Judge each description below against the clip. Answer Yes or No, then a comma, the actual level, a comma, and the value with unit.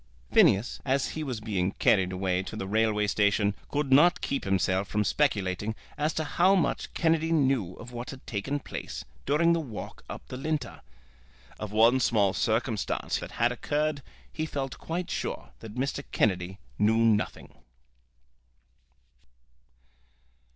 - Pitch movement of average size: No, wide, 6.0 semitones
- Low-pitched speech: Yes, low, 115 Hz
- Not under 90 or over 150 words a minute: Yes, average, 145 wpm